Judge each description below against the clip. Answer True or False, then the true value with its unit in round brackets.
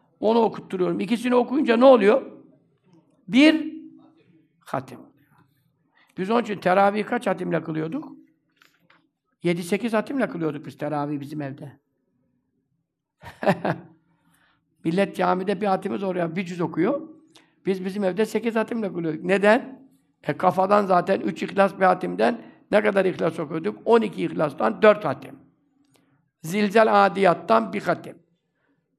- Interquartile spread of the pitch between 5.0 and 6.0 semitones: True (5.4 semitones)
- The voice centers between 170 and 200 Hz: True (190 Hz)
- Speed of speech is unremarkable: True (115 wpm)